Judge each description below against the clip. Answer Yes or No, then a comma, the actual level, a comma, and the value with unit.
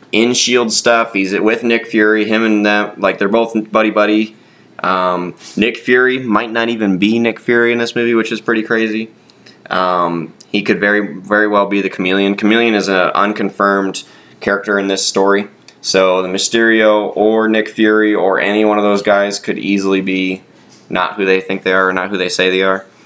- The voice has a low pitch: Yes, low, 105 Hz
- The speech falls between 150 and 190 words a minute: No, average, 200 wpm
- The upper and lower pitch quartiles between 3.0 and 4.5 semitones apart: No, narrow, 2.5 semitones